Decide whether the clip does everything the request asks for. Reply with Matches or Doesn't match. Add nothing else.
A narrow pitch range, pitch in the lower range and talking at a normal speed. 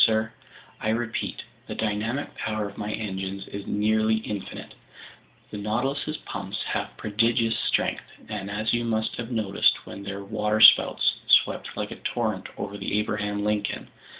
Matches